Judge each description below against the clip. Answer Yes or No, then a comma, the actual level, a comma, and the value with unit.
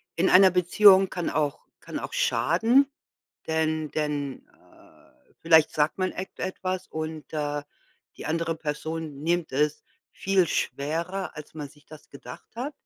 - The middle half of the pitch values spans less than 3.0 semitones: No, average, 3.7 semitones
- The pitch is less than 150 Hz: No, medium, 160 Hz